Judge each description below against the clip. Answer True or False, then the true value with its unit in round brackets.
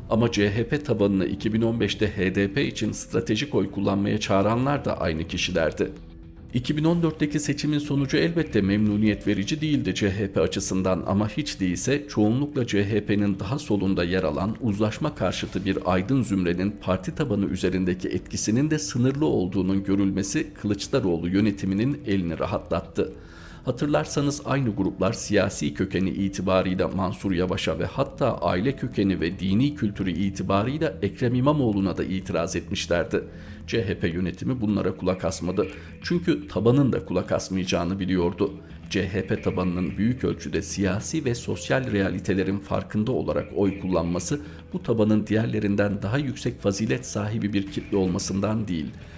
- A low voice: True (100 Hz)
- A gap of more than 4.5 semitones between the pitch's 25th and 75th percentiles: False (3.8 semitones)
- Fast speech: False (125 wpm)